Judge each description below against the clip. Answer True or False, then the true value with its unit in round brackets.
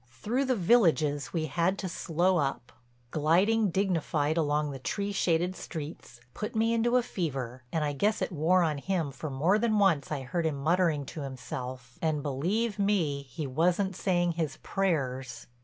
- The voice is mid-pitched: True (165 Hz)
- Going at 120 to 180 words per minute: True (175 wpm)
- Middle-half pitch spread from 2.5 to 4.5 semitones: False (5.1 semitones)